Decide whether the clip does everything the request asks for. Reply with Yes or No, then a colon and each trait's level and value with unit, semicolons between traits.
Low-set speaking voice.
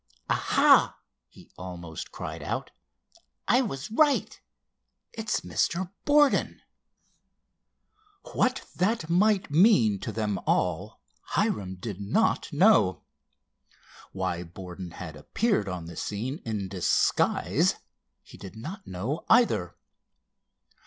Yes: low, 105 Hz